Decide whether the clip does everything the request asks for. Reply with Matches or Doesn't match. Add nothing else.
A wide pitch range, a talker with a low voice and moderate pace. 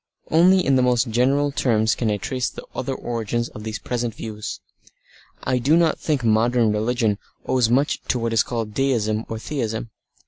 Doesn't match